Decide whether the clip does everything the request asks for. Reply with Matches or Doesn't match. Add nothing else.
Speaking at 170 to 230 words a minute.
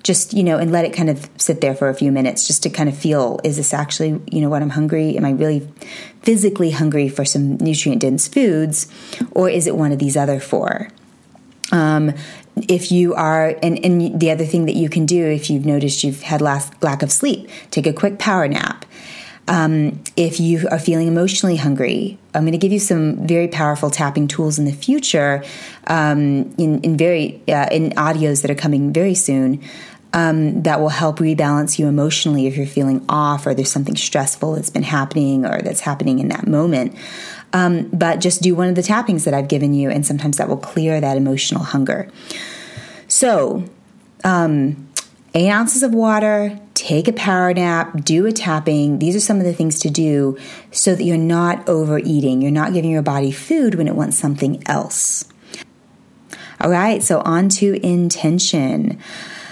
Matches